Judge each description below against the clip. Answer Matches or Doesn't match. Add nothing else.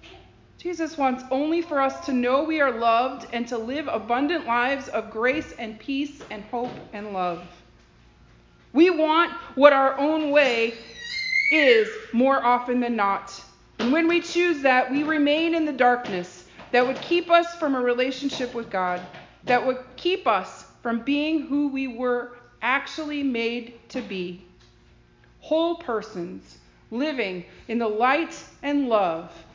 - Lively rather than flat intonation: Doesn't match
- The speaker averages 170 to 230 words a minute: Doesn't match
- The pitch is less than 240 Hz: Doesn't match